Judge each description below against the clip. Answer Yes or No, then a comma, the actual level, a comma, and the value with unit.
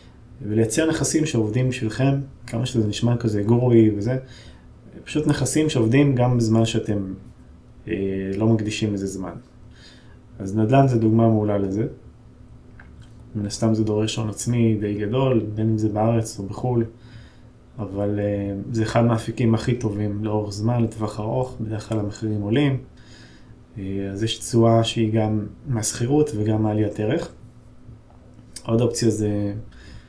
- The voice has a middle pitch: No, low, 110 Hz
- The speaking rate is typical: Yes, average, 140 wpm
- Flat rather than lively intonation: Yes, narrow, 2.1 semitones